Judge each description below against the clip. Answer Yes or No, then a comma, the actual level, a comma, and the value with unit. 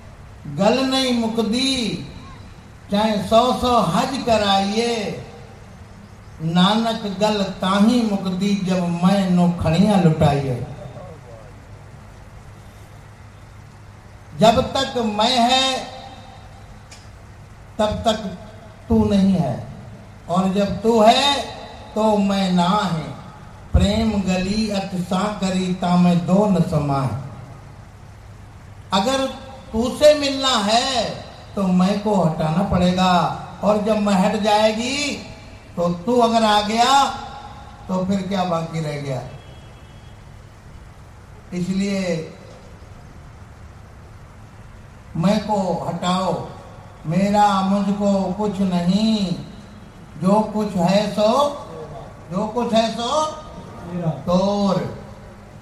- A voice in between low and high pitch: Yes, medium, 180 Hz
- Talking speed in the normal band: No, slow, 95 wpm